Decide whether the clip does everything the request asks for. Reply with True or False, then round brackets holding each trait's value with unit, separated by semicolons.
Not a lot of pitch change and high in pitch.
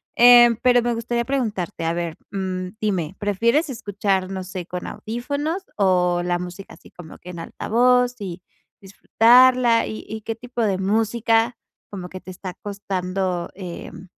False (4.5 semitones; 205 Hz)